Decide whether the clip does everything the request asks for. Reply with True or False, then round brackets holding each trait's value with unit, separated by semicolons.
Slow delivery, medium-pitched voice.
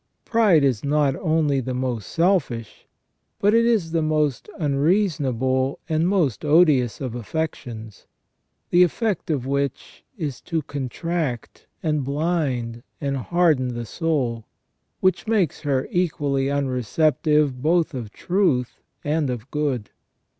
True (125 wpm; 145 Hz)